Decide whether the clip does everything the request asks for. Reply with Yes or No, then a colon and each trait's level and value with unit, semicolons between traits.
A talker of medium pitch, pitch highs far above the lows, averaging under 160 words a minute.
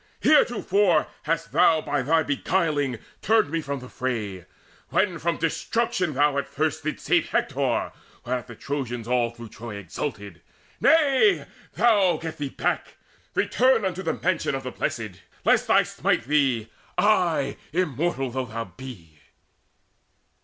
Yes: medium, 145 Hz; wide, 6.1 semitones; average, 145 wpm